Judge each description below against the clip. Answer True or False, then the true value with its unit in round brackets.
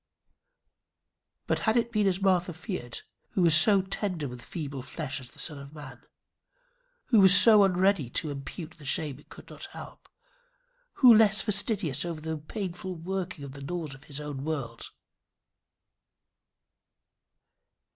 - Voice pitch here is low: False (165 Hz)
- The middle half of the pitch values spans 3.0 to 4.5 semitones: False (5.3 semitones)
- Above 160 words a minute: False (145 wpm)